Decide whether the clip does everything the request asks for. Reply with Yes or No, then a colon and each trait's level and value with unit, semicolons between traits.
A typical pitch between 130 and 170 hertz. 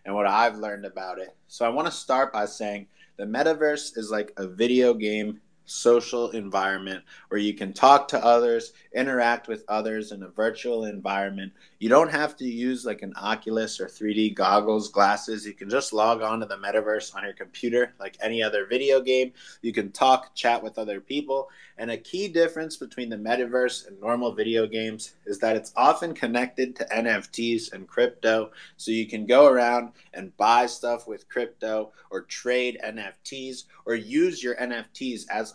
No: low, 115 Hz